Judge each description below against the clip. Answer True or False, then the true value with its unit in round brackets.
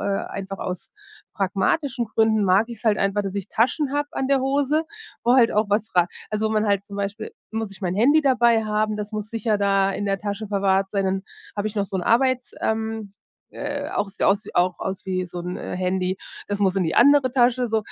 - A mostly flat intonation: False (3.2 semitones)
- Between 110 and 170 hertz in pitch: False (210 Hz)